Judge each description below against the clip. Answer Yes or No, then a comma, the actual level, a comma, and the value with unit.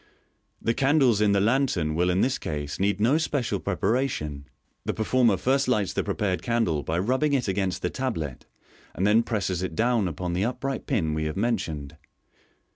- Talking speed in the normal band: Yes, average, 180 wpm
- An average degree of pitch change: No, wide, 6.0 semitones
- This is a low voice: Yes, low, 100 Hz